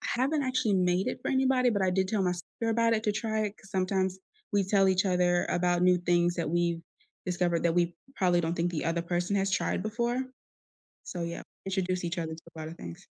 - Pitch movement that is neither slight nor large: Yes, average, 3.1 semitones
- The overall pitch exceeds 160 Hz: Yes, medium, 185 Hz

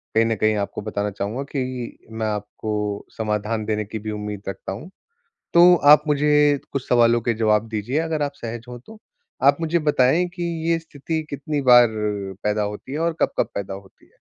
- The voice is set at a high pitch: No, low, 120 Hz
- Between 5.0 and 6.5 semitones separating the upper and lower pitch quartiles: Yes, wide, 5.6 semitones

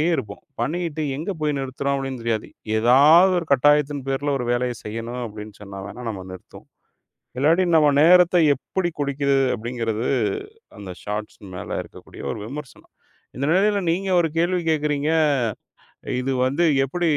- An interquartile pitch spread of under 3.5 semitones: No, average, 5.1 semitones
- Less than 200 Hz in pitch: Yes, medium, 140 Hz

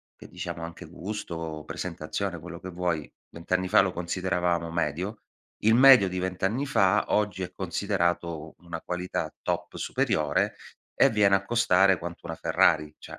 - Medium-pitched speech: No, very low, 90 Hz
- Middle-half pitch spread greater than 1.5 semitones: Yes, narrow, 2.6 semitones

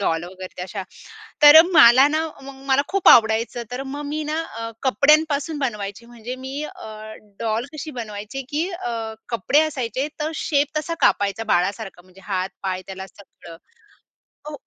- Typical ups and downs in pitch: No, wide, 6.3 semitones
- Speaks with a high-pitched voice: Yes, high, 240 Hz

